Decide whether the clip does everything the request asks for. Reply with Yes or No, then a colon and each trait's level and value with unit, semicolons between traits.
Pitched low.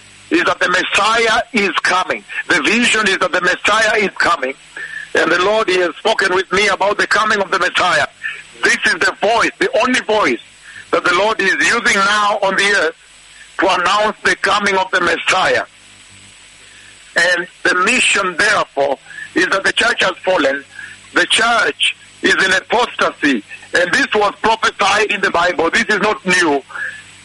No: high, 210 Hz